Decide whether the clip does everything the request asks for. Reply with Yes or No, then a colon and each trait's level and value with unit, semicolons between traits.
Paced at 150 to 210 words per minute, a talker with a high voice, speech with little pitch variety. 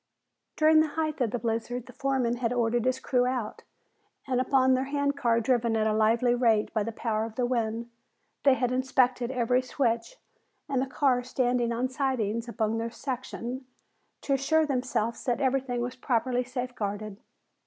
Yes: average, 170 wpm; very high, 250 Hz; narrow, 2.2 semitones